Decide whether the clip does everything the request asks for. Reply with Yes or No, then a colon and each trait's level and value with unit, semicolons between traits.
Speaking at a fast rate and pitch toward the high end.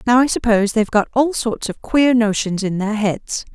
Yes: fast, 220 wpm; high, 225 Hz